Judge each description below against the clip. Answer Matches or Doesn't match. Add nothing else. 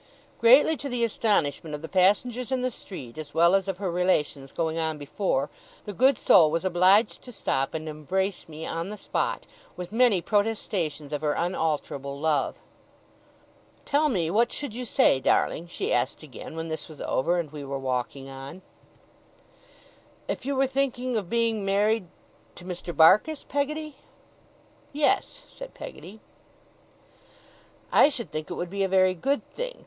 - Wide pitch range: Matches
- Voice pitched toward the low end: Doesn't match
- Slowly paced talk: Doesn't match